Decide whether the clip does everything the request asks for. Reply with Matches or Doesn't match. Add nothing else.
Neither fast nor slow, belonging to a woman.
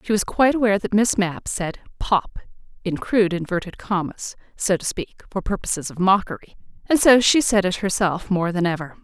Matches